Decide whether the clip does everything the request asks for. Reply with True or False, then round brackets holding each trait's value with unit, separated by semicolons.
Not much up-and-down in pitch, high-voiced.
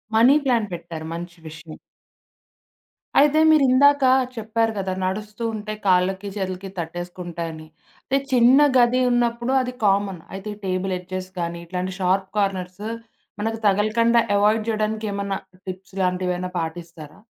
False (3.7 semitones; 195 Hz)